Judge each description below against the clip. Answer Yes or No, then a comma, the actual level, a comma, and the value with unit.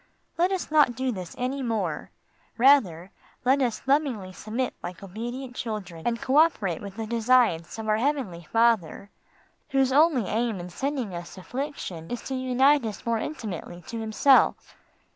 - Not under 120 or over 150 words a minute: No, average, 160 wpm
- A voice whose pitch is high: Yes, high, 235 Hz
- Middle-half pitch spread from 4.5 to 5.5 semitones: Yes, average, 5.2 semitones